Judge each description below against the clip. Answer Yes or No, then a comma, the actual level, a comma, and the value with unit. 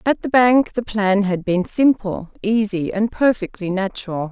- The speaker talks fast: No, average, 165 wpm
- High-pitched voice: Yes, high, 210 Hz